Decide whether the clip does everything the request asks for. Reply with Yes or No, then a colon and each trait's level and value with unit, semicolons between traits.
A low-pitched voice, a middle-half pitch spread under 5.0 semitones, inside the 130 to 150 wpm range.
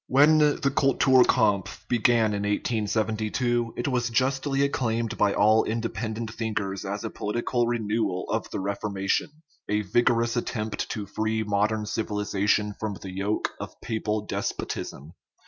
Yes: low, 110 Hz; narrow, 2.6 semitones; slow, 135 wpm